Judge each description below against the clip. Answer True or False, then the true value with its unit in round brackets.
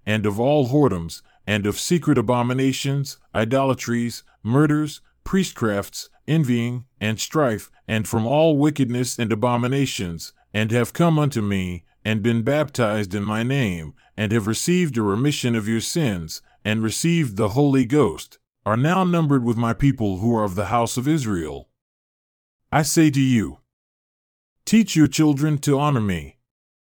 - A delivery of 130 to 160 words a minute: True (150 wpm)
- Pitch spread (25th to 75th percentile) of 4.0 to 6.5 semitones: True (5.2 semitones)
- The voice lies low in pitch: True (120 Hz)